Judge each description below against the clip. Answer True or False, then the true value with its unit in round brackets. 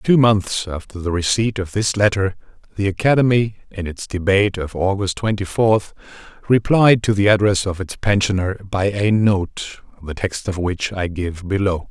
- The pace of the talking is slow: False (170 wpm)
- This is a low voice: True (100 Hz)